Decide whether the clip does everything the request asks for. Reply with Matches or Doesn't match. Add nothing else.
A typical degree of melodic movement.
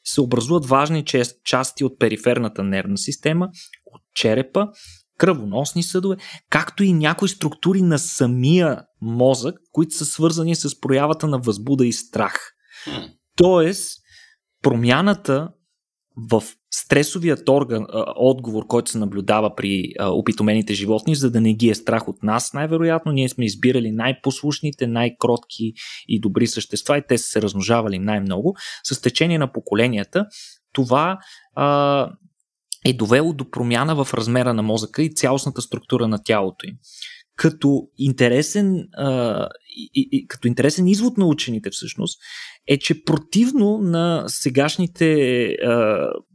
Doesn't match